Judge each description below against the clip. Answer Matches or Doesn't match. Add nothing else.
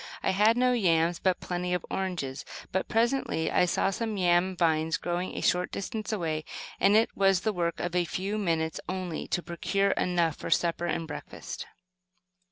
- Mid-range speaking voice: Matches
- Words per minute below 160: Doesn't match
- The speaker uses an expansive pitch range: Doesn't match